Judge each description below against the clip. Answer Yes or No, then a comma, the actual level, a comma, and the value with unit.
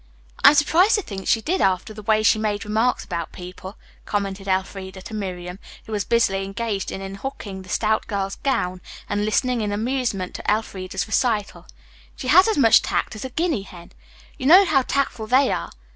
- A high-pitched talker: Yes, high, 210 Hz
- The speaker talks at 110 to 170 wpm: No, average, 190 wpm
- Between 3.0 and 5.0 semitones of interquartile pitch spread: Yes, average, 4.6 semitones